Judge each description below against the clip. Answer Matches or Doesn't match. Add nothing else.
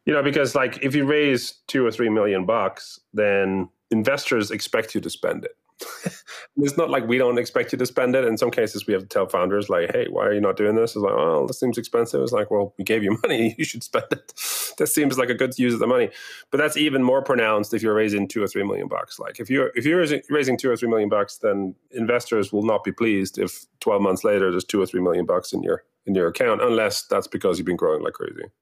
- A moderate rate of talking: Doesn't match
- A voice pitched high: Doesn't match